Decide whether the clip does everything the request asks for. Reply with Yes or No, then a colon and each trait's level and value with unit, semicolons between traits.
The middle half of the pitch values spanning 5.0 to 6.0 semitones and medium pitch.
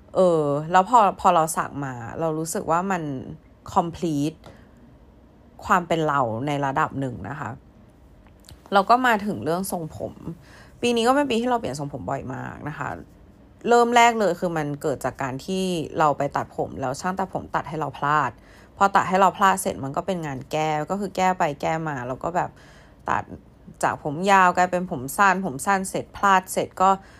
Yes: wide, 5.4 semitones; medium, 165 Hz